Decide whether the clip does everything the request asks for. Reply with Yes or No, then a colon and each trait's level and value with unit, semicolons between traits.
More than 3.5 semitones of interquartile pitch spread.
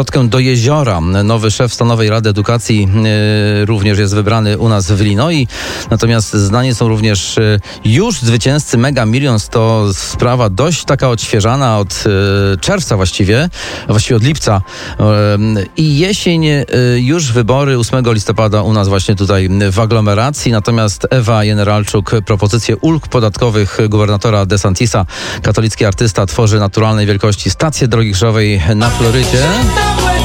No: average, 2.9 semitones